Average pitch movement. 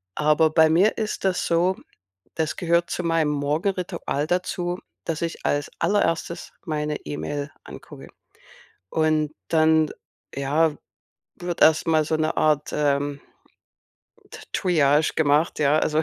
No: narrow, 2.3 semitones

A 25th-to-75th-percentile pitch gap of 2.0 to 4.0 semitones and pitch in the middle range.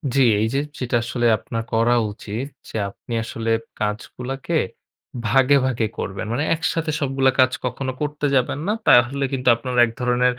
No: average, 2.7 semitones; low, 125 Hz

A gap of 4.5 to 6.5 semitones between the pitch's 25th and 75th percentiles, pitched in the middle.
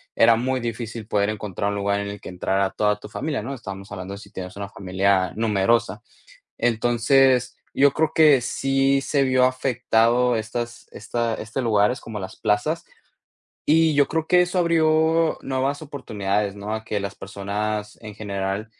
No: average, 4.8 semitones; low, 115 Hz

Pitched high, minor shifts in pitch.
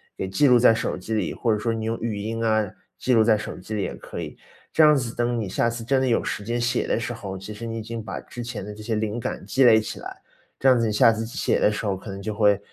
No: low, 115 Hz; narrow, 2.0 semitones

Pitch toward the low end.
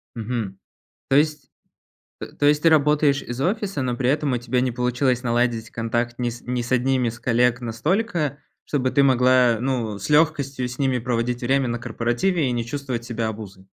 Yes: low, 125 Hz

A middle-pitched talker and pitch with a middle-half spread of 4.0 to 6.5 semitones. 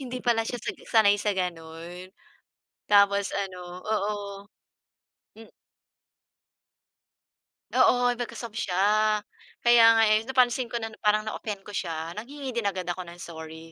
No: high, 210 Hz; average, 4.6 semitones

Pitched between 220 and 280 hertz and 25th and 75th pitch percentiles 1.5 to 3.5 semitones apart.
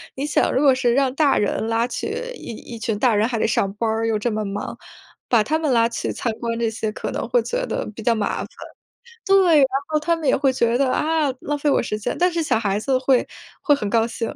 No: high, 240 Hz; average, 4.7 semitones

